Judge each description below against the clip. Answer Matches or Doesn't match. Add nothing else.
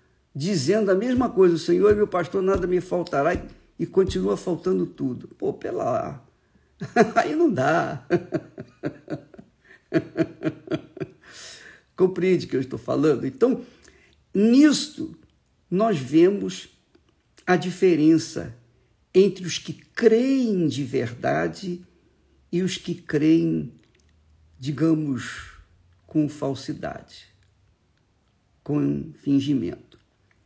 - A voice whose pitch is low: Doesn't match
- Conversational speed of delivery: Doesn't match